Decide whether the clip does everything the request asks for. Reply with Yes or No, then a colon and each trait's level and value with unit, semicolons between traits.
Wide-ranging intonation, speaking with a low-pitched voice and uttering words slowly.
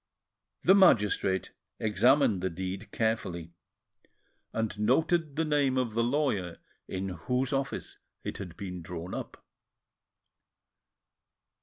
Yes: wide, 6.4 semitones; low, 110 Hz; slow, 110 wpm